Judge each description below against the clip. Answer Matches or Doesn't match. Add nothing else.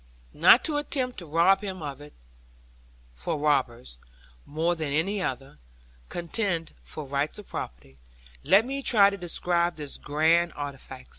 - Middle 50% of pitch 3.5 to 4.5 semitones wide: Doesn't match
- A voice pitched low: Doesn't match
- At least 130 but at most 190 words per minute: Matches